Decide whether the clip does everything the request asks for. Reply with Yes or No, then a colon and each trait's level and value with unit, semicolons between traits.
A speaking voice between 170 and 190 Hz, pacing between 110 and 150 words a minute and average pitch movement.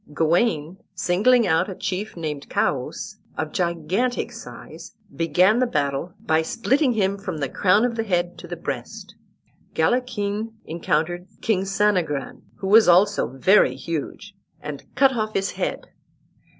Yes: medium, 185 Hz; average, 140 wpm; average, 5.0 semitones